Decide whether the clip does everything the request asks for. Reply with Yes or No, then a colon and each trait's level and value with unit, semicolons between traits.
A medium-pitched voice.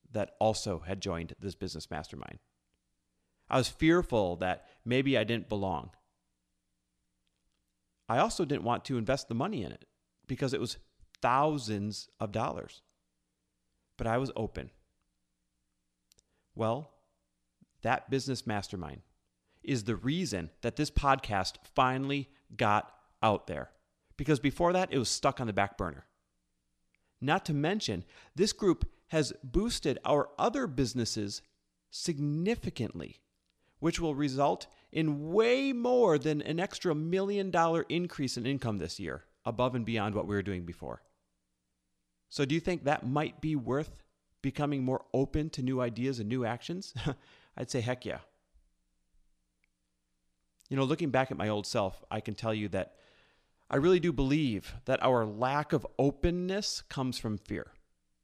No: low, 115 Hz